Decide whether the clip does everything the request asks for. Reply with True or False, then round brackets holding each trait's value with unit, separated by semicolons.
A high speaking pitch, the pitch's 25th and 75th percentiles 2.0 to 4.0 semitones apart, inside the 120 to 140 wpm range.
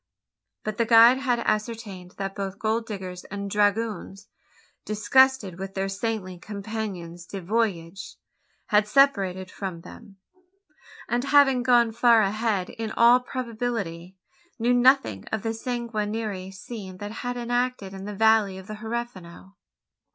True (215 Hz; 3.4 semitones; 135 wpm)